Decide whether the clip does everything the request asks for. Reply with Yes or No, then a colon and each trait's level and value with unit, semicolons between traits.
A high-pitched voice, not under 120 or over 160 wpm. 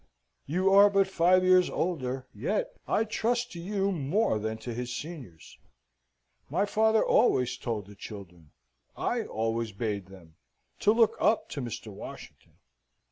No: medium, 140 Hz; average, 145 wpm